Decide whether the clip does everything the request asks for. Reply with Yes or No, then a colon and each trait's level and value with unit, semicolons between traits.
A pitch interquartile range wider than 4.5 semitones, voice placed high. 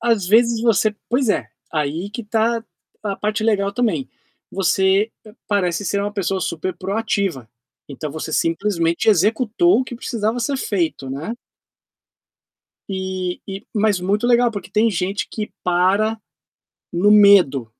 No: average, 3.5 semitones; high, 200 Hz